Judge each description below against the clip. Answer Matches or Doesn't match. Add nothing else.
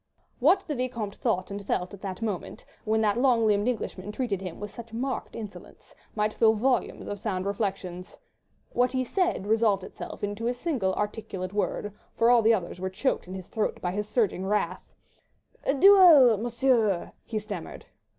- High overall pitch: Matches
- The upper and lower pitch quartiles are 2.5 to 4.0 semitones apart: Matches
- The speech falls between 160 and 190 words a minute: Matches